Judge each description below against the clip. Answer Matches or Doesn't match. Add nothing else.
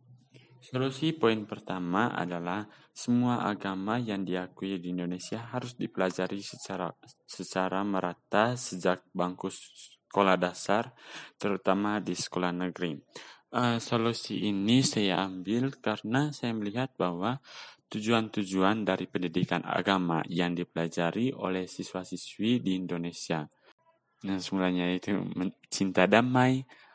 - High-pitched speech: Doesn't match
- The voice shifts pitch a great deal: Doesn't match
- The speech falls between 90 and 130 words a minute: Matches